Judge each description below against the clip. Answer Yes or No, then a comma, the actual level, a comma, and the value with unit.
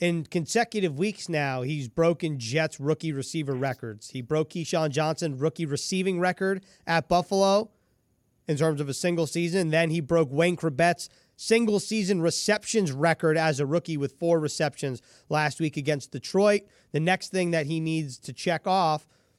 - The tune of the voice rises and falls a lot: No, average, 3.1 semitones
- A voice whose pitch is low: No, medium, 160 Hz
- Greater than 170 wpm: No, average, 165 wpm